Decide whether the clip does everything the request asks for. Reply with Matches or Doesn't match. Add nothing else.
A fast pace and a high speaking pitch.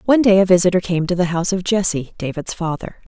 Doesn't match